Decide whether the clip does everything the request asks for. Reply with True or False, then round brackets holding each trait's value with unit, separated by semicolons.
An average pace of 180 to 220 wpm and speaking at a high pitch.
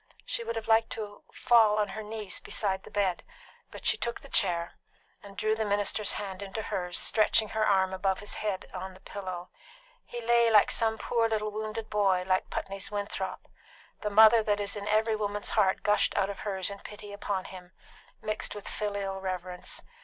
True (190 wpm; 205 Hz)